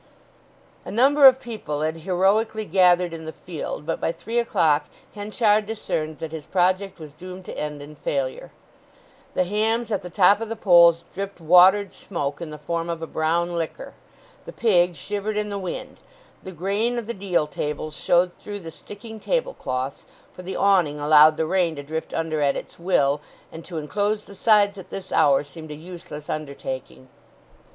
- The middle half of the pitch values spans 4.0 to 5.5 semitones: Yes, average, 4.7 semitones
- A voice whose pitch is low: No, medium, 175 Hz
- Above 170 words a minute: Yes, average, 180 wpm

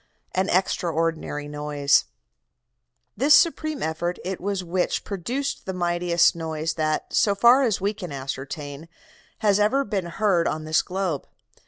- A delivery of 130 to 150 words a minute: Yes, average, 140 wpm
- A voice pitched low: No, medium, 175 Hz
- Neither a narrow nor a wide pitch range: Yes, average, 4.3 semitones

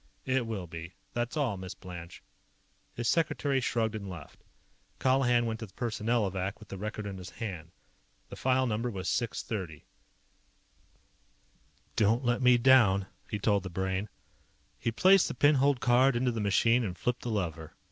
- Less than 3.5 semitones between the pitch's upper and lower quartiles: No, average, 4.4 semitones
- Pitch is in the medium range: No, low, 110 Hz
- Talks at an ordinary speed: Yes, average, 165 wpm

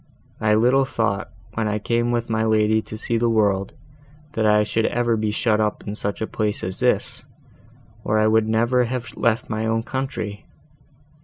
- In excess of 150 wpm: Yes, average, 185 wpm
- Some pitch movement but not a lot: No, narrow, 1.6 semitones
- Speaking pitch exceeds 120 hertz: No, low, 110 Hz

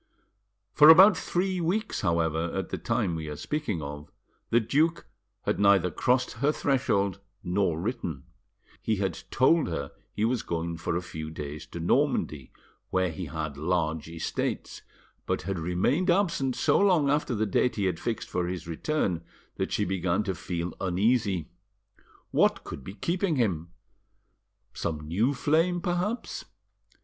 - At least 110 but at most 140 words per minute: No, average, 155 wpm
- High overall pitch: No, very low, 95 Hz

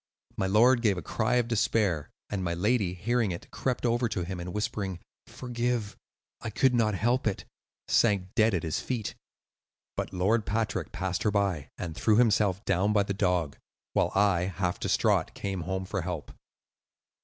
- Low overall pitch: Yes, low, 100 Hz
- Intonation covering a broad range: No, average, 3.8 semitones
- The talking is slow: No, average, 175 wpm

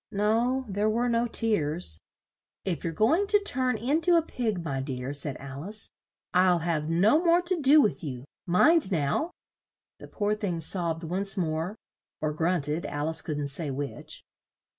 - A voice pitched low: No, medium, 185 Hz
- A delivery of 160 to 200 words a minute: Yes, average, 175 wpm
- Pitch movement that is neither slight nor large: No, wide, 7.2 semitones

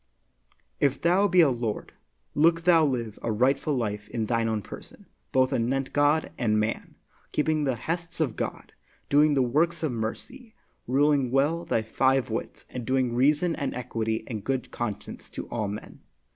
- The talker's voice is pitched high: No, low, 130 Hz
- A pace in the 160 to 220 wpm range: Yes, average, 170 wpm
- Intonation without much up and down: No, average, 4.9 semitones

